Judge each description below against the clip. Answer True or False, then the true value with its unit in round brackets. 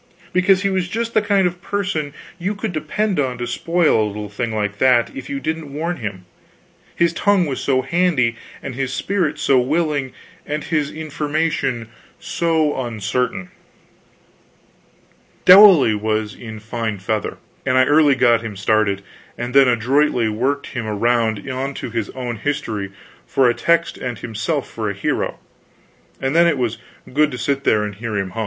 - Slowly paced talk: False (170 wpm)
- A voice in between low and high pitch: False (130 Hz)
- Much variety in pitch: True (5.9 semitones)